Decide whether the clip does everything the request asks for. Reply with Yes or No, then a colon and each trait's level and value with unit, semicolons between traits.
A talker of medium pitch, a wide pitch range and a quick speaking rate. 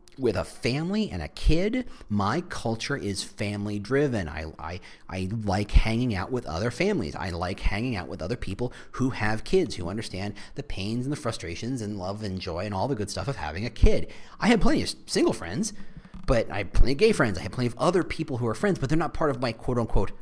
No: low, 115 Hz; wide, 6.0 semitones; fast, 235 wpm